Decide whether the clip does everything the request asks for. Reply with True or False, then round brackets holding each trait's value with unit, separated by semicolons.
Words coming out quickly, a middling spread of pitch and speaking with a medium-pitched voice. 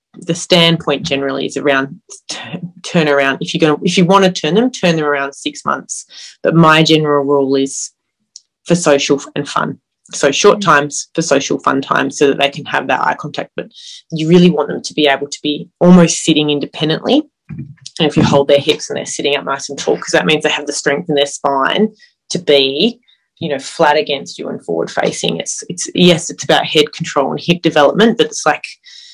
True (215 wpm; 3.4 semitones; 150 Hz)